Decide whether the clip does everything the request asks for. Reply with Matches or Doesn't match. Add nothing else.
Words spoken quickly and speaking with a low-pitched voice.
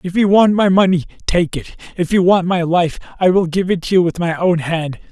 Doesn't match